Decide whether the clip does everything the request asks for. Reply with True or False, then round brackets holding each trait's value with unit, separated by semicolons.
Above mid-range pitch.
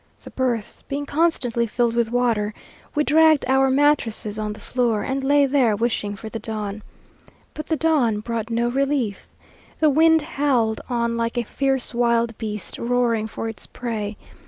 True (240 Hz)